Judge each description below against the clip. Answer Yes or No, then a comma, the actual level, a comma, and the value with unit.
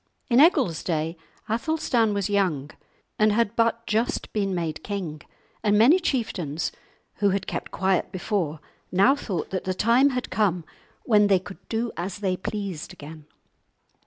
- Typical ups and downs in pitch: Yes, average, 4.4 semitones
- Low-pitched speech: No, high, 200 Hz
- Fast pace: No, average, 155 wpm